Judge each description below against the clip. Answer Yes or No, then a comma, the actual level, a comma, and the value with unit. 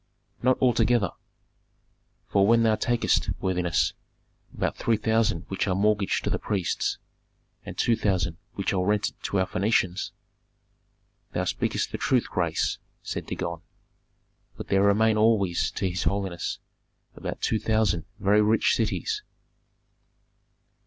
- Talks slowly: Yes, slow, 130 wpm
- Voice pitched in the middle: No, low, 100 Hz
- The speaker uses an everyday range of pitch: Yes, average, 3.1 semitones